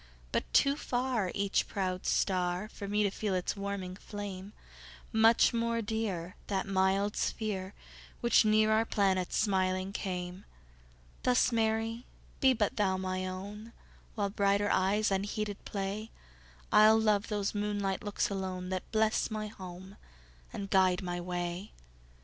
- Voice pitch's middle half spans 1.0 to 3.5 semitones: Yes, narrow, 2.5 semitones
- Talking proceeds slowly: Yes, slow, 115 wpm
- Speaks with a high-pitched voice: Yes, high, 200 Hz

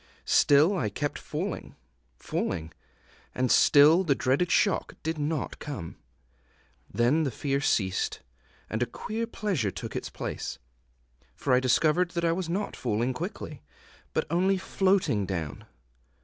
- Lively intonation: Yes, wide, 6.6 semitones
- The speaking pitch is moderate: Yes, medium, 145 Hz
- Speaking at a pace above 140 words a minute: No, slow, 135 wpm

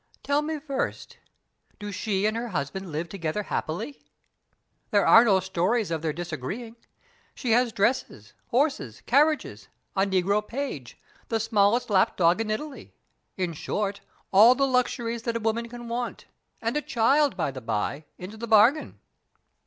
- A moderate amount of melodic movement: Yes, average, 4.9 semitones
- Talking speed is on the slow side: No, average, 155 wpm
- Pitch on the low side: No, high, 215 Hz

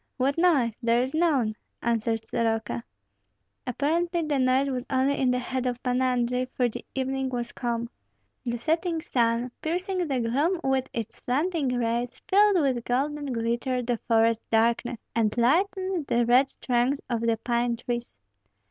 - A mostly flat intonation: No, average, 3.1 semitones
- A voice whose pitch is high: Yes, very high, 250 Hz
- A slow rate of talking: No, average, 155 wpm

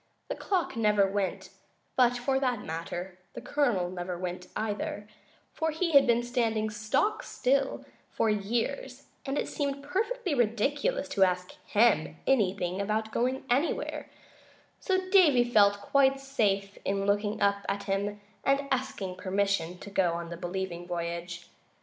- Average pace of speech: Yes, average, 145 wpm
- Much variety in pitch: Yes, wide, 6.0 semitones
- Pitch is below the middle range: No, high, 210 Hz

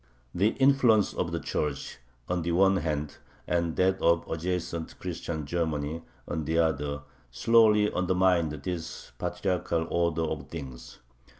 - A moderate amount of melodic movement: Yes, average, 3.0 semitones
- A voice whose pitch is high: No, very low, 85 Hz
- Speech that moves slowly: Yes, slow, 130 wpm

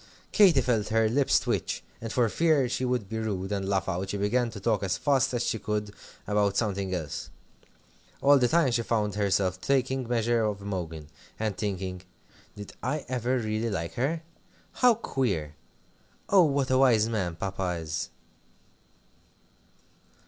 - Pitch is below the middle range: Yes, low, 110 Hz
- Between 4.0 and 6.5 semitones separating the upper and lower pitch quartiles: Yes, average, 4.6 semitones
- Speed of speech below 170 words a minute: Yes, average, 160 wpm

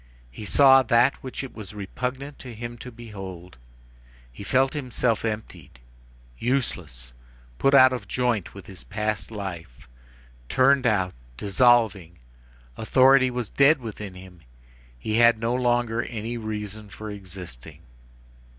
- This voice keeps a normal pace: No, slow, 130 wpm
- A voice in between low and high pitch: No, low, 110 Hz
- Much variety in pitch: No, average, 4.3 semitones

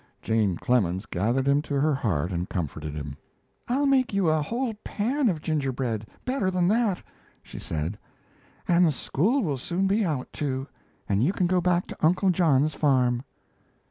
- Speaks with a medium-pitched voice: Yes, medium, 150 Hz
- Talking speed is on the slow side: No, average, 170 wpm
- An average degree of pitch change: No, wide, 8.5 semitones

